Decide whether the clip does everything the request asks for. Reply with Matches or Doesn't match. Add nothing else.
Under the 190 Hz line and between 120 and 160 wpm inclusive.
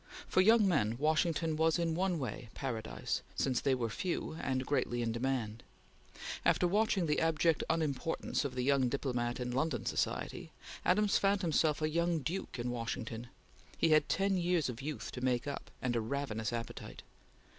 Doesn't match